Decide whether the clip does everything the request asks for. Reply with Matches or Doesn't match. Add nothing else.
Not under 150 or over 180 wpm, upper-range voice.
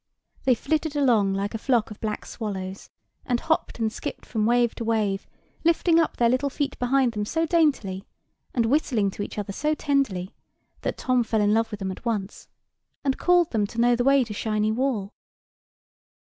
Doesn't match